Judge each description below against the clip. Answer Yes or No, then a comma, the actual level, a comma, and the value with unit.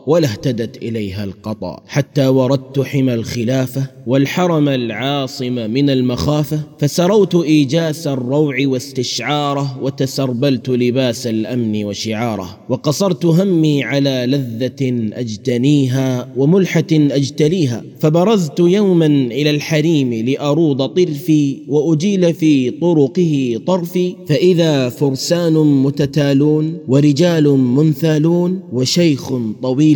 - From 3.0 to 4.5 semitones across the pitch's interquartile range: Yes, average, 3.5 semitones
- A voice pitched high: No, medium, 140 Hz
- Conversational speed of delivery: Yes, average, 90 wpm